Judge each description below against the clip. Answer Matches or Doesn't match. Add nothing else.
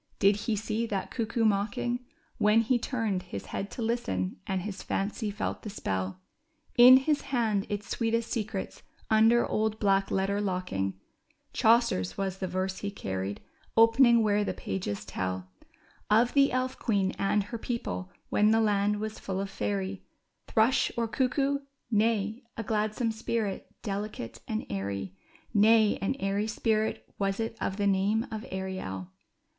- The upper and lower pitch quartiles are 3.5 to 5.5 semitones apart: Doesn't match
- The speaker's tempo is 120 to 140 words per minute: Doesn't match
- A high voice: Matches